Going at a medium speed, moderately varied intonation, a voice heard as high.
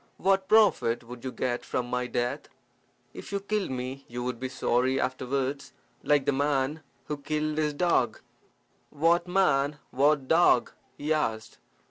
No: average, 150 wpm; average, 3.6 semitones; medium, 140 Hz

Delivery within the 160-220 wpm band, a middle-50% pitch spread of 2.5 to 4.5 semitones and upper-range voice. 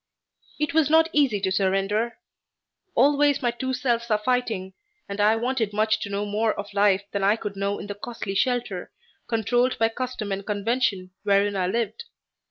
Yes: average, 180 wpm; average, 3.6 semitones; high, 215 Hz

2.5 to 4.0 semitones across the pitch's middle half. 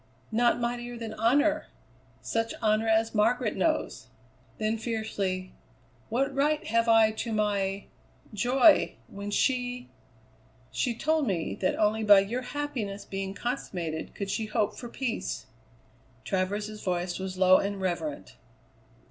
Yes: average, 3.6 semitones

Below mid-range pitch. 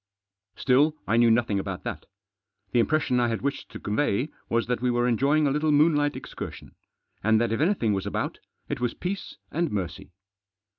Yes: low, 125 Hz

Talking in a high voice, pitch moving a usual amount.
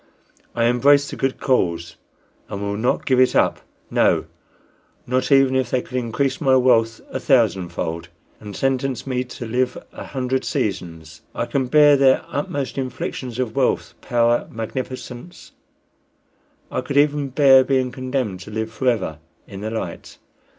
No: low, 125 Hz; average, 3.0 semitones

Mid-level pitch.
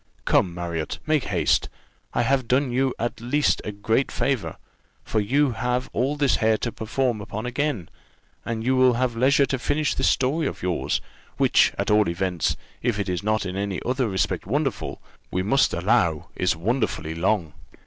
No: low, 115 Hz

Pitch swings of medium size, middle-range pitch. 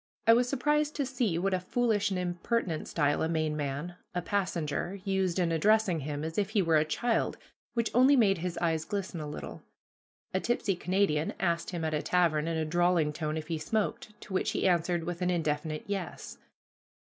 Yes: average, 4.2 semitones; medium, 175 Hz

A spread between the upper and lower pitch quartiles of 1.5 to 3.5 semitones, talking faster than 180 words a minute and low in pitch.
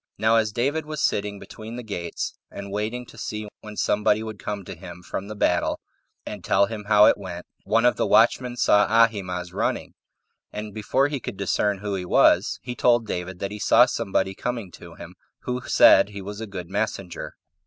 Yes: average, 2.7 semitones; fast, 205 wpm; low, 105 Hz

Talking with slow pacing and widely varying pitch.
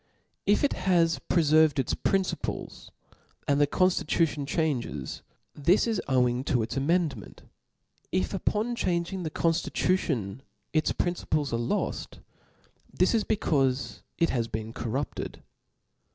Yes: slow, 125 wpm; wide, 5.8 semitones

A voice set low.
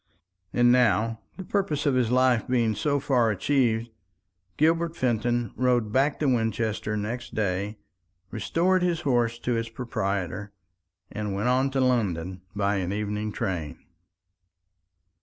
Yes: low, 115 Hz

